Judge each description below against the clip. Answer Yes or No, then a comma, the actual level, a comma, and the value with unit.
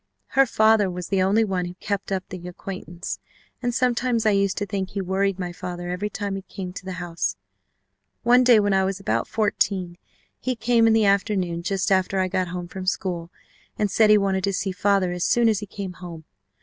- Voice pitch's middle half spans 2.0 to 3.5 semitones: Yes, narrow, 2.6 semitones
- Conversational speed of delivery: No, fast, 215 wpm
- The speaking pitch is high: Yes, high, 195 Hz